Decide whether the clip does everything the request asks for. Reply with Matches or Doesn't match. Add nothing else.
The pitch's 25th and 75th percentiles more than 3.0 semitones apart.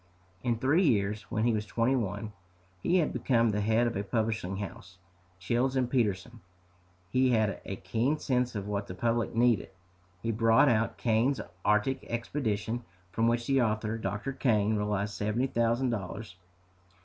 Doesn't match